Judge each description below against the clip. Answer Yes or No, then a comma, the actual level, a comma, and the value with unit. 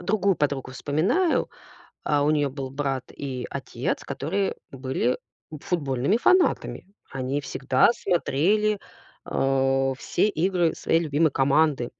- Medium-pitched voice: Yes, medium, 145 Hz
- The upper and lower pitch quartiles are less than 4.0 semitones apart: No, average, 4.9 semitones